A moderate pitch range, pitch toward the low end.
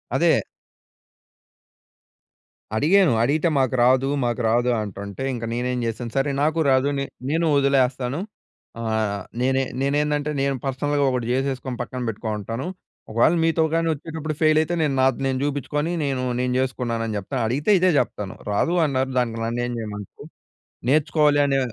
Yes: average, 3.6 semitones; low, 130 Hz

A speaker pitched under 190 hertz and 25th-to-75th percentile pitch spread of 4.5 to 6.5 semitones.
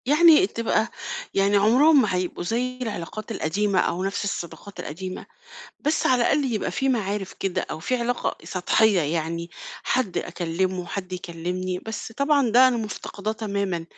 No: high, 205 Hz; average, 4.9 semitones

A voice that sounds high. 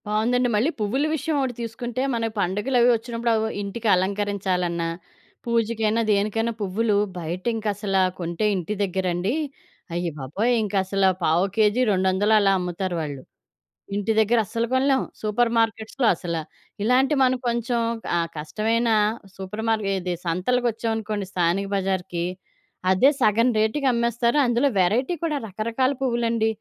Yes: high, 215 Hz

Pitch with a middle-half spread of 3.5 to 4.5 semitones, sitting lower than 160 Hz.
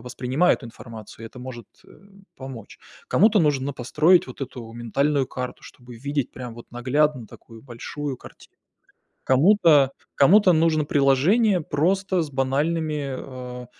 Yes: average, 3.9 semitones; low, 135 Hz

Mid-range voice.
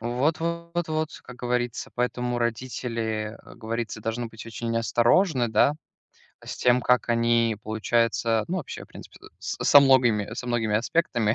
No: low, 120 Hz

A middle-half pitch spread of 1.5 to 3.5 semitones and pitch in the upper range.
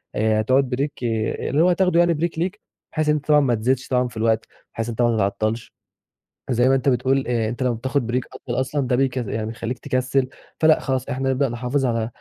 No: average, 3.1 semitones; low, 130 Hz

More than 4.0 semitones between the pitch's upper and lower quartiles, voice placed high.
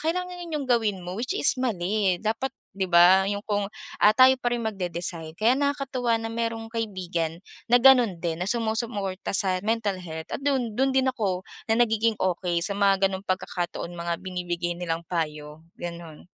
Yes: average, 5.0 semitones; high, 200 Hz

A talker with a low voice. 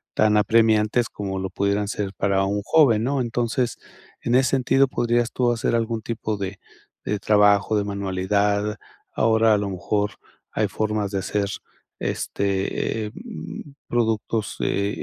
Yes: low, 105 Hz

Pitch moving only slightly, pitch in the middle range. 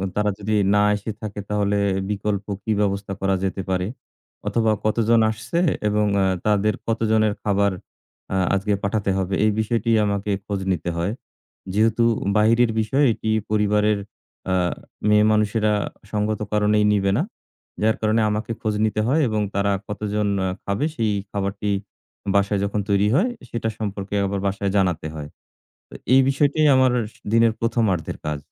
No: narrow, 1.6 semitones; low, 105 Hz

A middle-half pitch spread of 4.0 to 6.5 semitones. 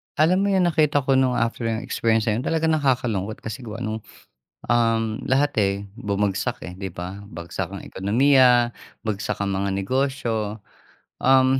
Yes: average, 4.4 semitones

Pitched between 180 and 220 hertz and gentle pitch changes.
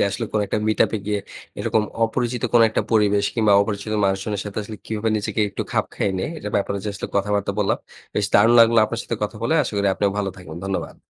No: low, 105 Hz; narrow, 1.8 semitones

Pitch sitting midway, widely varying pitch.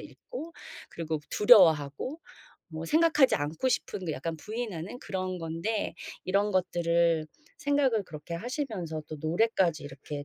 Yes: medium, 180 Hz; wide, 6.1 semitones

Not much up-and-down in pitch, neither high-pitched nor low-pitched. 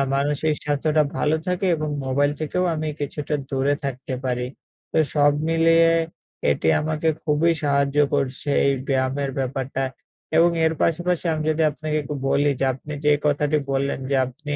Yes: narrow, 2.2 semitones; medium, 145 Hz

